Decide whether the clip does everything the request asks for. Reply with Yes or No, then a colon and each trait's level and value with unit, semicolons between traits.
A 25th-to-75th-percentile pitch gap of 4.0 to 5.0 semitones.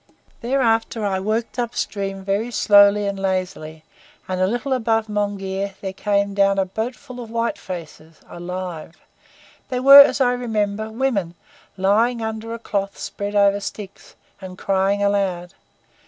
No: average, 2.9 semitones